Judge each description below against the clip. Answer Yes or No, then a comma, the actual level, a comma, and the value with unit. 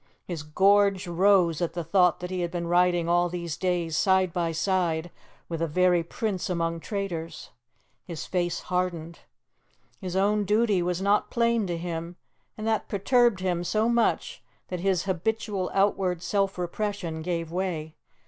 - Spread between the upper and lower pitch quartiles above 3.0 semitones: No, average, 2.7 semitones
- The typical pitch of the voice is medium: Yes, medium, 180 Hz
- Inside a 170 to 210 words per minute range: No, average, 160 wpm